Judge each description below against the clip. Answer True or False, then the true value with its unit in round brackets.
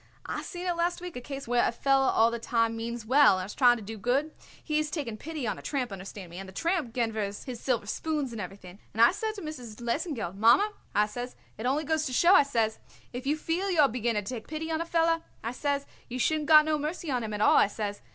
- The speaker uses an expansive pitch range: True (5.7 semitones)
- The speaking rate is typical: False (265 wpm)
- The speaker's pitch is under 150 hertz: False (250 Hz)